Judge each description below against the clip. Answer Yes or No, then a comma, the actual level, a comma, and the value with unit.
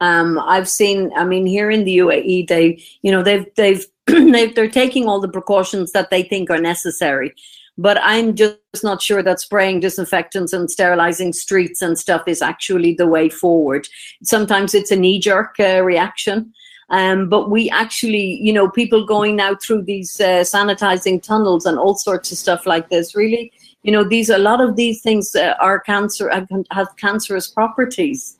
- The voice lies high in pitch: Yes, high, 195 Hz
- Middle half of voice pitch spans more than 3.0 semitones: No, narrow, 2.6 semitones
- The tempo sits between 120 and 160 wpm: No, average, 180 wpm